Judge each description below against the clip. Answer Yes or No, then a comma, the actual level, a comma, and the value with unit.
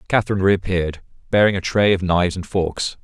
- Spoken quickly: No, average, 180 wpm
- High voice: No, very low, 95 Hz